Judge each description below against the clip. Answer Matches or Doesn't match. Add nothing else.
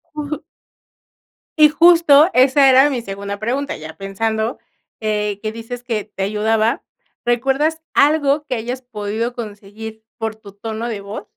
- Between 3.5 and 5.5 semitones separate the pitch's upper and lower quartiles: Matches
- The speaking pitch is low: Doesn't match